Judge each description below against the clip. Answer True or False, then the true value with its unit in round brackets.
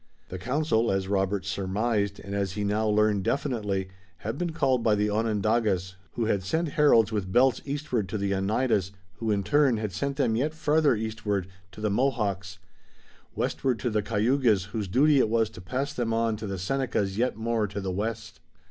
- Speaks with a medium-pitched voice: False (110 Hz)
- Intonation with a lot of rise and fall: False (4.0 semitones)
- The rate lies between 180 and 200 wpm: True (190 wpm)